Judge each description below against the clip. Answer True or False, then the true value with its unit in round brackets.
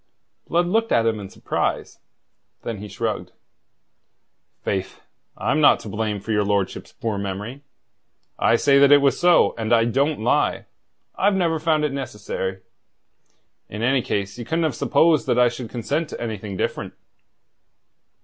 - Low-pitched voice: True (120 Hz)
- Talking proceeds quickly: False (160 wpm)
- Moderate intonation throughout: False (6.2 semitones)